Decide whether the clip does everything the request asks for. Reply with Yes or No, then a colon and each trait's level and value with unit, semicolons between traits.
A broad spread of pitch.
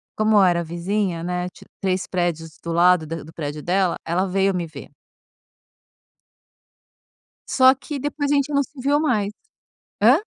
Yes: wide, 6.8 semitones